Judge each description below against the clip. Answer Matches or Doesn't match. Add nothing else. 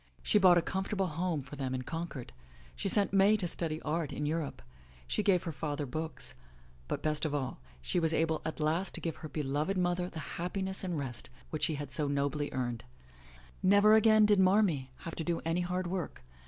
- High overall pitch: Doesn't match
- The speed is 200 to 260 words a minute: Matches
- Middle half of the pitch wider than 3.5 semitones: Matches